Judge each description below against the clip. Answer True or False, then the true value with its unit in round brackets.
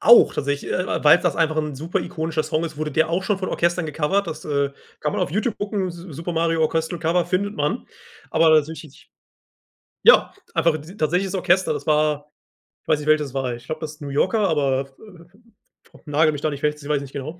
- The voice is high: False (155 Hz)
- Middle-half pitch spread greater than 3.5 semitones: False (2.7 semitones)